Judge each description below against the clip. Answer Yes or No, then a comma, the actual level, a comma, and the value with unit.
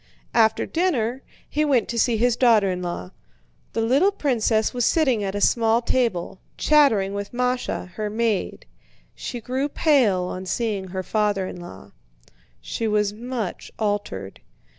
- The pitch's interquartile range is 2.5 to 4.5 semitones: Yes, average, 3.9 semitones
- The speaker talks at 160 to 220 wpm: No, average, 150 wpm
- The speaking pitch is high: Yes, high, 225 Hz